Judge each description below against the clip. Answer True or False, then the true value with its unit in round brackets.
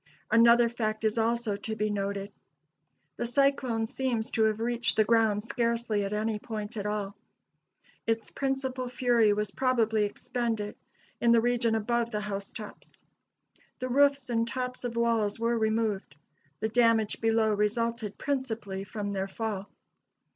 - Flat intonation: True (2.1 semitones)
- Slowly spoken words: False (145 wpm)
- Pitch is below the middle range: False (225 Hz)